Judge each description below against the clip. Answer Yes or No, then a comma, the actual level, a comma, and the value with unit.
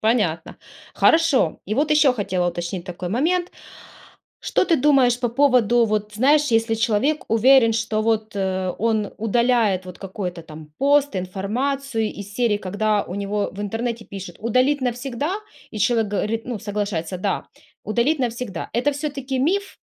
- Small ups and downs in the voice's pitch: No, average, 4.5 semitones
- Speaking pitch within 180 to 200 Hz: No, high, 225 Hz